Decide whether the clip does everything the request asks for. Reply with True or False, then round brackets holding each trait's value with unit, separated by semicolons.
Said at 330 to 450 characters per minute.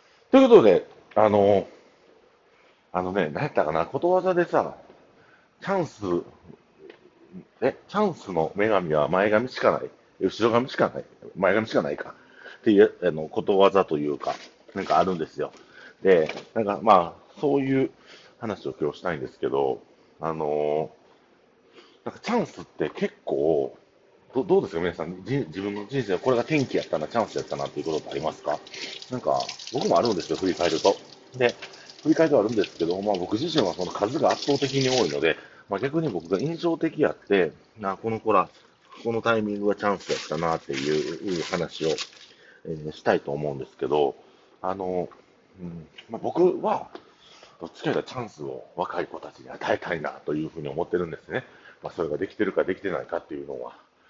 True (355 characters per minute)